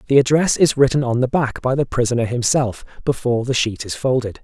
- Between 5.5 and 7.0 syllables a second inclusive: Yes, 5.9 syllables/s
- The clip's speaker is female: No, male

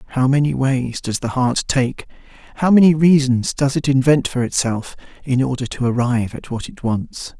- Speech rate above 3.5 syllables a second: Yes, 5.0 syllables/s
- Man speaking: Yes, male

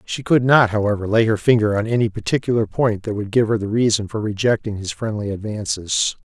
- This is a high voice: No, low, 110 Hz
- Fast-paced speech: Yes, fast, 210 wpm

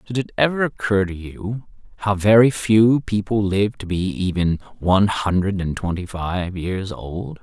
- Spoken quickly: No, average, 170 wpm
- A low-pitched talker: Yes, low, 100 Hz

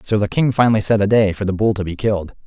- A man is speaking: Yes, male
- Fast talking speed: Yes, fast, 315 wpm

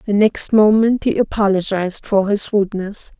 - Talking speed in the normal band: Yes, average, 150 wpm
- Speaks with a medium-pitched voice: No, high, 205 Hz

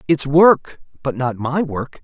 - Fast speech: No, average, 150 wpm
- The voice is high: No, medium, 145 Hz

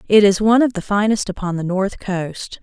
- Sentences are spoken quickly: Yes, fast, 230 wpm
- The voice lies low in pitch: No, high, 200 Hz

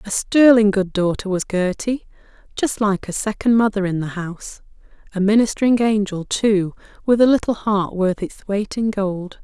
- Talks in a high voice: Yes, high, 205 Hz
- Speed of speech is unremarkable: Yes, average, 170 wpm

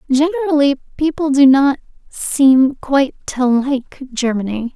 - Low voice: No, very high, 275 Hz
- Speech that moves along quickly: No, slow, 115 wpm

